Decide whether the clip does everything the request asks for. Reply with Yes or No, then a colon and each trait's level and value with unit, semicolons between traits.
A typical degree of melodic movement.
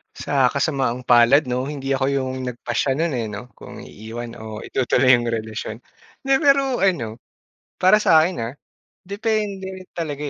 No: wide, 6.8 semitones